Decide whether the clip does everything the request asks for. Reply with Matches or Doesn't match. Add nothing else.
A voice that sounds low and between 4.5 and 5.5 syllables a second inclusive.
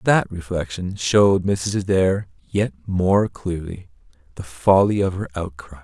Doesn't match